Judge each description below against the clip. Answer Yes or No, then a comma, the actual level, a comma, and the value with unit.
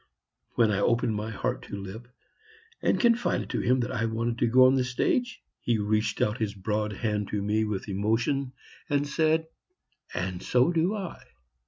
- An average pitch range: Yes, average, 3.7 semitones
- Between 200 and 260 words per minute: No, average, 180 wpm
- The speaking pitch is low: Yes, low, 115 Hz